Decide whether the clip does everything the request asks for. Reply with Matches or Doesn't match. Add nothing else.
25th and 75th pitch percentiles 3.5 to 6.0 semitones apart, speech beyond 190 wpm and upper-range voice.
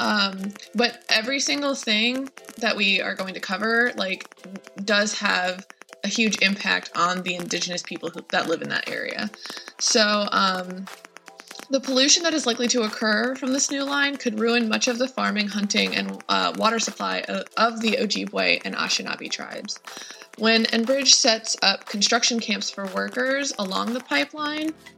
Doesn't match